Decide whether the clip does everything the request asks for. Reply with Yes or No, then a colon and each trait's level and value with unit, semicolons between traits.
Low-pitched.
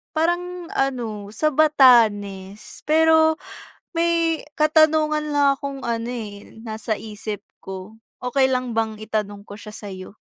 No: high, 245 Hz